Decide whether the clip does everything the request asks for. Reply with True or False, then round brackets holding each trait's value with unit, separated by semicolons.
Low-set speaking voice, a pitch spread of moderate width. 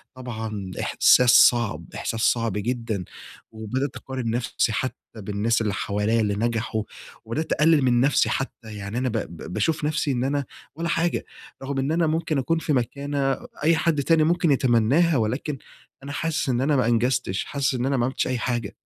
True (125 Hz; 4.2 semitones)